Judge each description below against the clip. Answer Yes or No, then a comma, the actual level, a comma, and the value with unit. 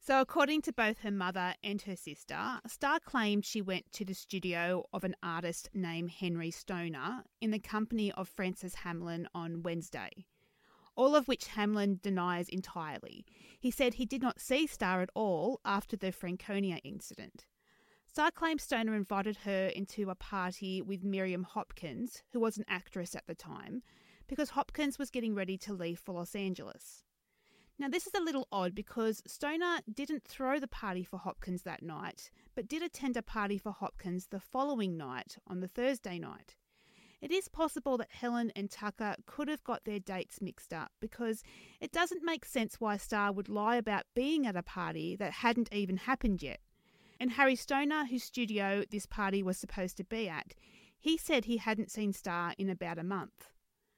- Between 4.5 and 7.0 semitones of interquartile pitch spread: Yes, average, 5.1 semitones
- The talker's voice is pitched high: Yes, high, 205 Hz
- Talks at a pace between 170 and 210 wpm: Yes, average, 180 wpm